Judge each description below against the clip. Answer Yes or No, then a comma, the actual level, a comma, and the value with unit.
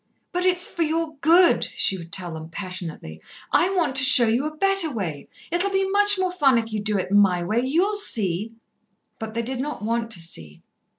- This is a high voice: Yes, high, 240 Hz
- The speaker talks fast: Yes, fast, 215 wpm